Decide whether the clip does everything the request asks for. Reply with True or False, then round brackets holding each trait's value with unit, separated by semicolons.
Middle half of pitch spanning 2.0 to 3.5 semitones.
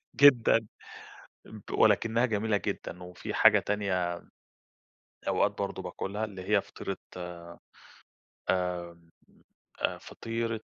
False (4.0 semitones)